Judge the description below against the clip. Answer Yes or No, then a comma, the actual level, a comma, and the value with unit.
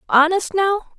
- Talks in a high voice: Yes, very high, 350 Hz